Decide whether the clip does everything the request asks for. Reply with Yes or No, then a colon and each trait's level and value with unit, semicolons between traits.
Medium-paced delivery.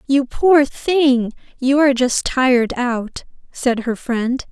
Yes: average, 145 wpm